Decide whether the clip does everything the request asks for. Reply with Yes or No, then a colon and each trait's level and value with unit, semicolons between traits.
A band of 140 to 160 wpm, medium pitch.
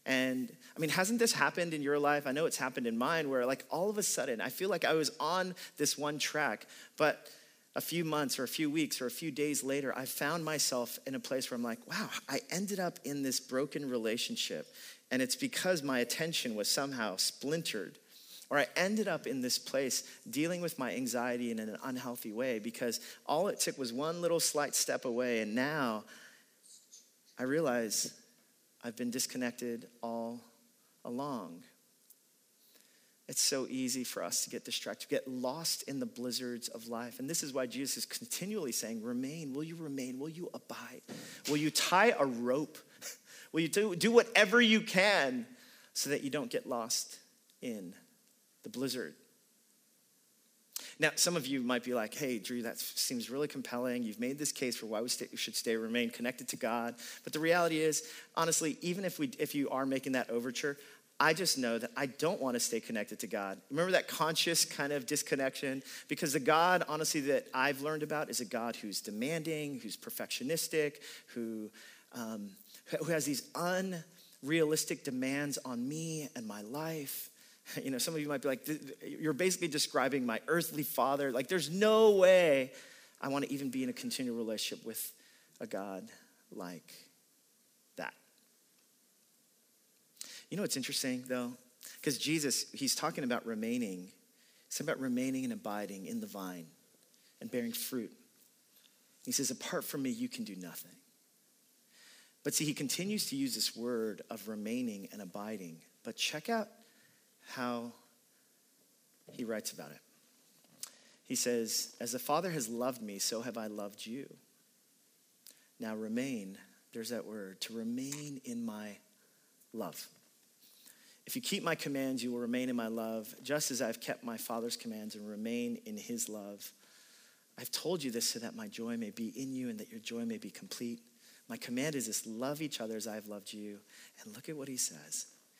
No: average, 180 wpm; medium, 150 Hz